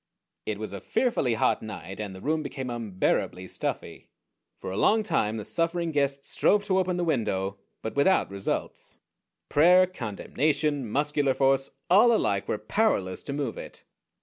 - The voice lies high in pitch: No, low, 135 Hz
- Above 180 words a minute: No, average, 160 wpm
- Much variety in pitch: Yes, wide, 8.0 semitones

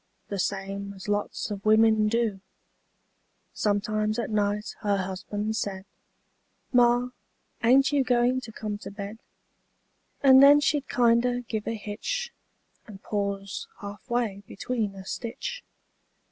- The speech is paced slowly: Yes, slow, 130 wpm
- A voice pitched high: Yes, high, 215 Hz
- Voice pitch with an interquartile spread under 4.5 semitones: Yes, average, 3.2 semitones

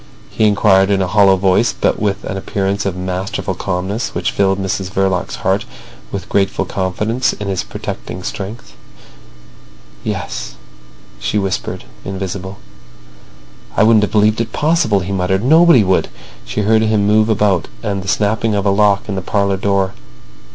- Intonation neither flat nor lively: No, narrow, 1.9 semitones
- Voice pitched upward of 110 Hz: No, low, 100 Hz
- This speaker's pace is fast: No, average, 160 wpm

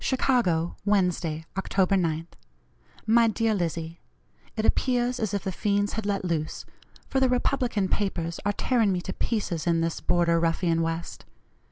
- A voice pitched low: No, high, 190 Hz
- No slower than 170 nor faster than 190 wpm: No, average, 155 wpm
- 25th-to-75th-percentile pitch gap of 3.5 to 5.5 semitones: Yes, average, 4.7 semitones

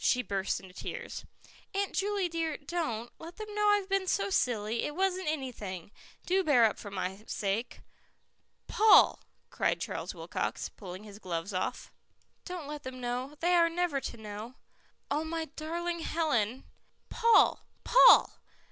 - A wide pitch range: Yes, wide, 8.5 semitones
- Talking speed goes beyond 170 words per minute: No, average, 155 wpm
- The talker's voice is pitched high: Yes, very high, 295 Hz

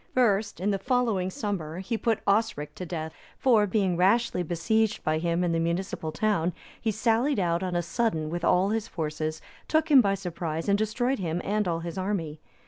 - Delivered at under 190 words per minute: No, average, 195 wpm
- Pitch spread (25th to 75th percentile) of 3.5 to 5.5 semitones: Yes, average, 4.5 semitones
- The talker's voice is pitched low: No, high, 190 Hz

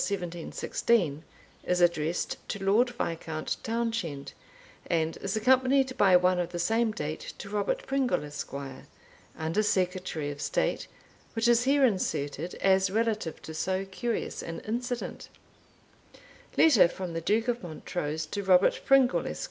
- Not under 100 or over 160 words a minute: Yes, average, 140 wpm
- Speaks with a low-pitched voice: No, high, 190 Hz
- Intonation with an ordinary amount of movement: No, wide, 5.7 semitones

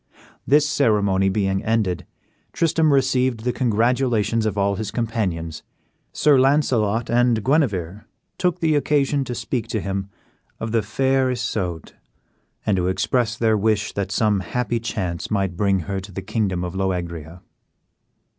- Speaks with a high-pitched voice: No, low, 110 Hz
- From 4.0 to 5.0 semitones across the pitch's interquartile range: Yes, average, 4.4 semitones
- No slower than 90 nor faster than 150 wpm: Yes, average, 145 wpm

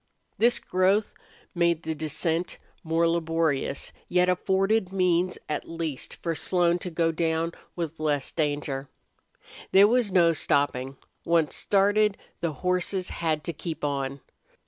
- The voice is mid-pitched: Yes, medium, 170 Hz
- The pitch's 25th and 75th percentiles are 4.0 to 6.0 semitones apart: No, average, 2.7 semitones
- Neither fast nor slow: No, slow, 130 wpm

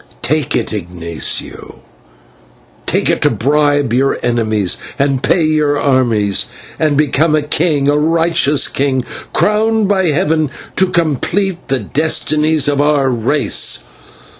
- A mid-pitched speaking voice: Yes, medium, 145 Hz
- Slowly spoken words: Yes, slow, 125 wpm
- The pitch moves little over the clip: No, average, 3.2 semitones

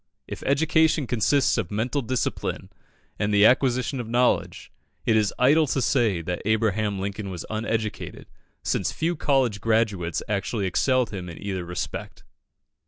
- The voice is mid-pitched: No, low, 110 Hz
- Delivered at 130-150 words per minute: Yes, average, 145 wpm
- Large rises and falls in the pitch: No, average, 4.2 semitones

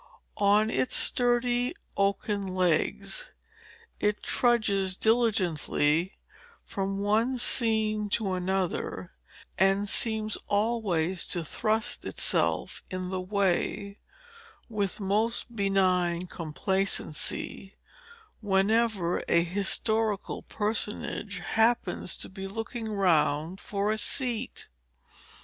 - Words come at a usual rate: No, slow, 90 wpm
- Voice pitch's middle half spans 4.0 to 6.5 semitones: No, average, 3.0 semitones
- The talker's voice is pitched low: No, high, 200 Hz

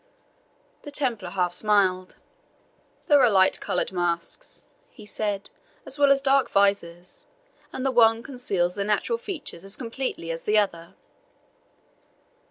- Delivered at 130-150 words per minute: Yes, slow, 135 wpm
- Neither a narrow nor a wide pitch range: No, wide, 6.2 semitones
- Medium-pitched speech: No, high, 210 Hz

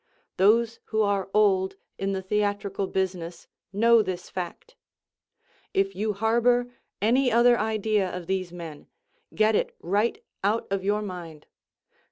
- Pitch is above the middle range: Yes, high, 200 Hz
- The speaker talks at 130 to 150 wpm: Yes, slow, 135 wpm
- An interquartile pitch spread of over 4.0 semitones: No, average, 2.7 semitones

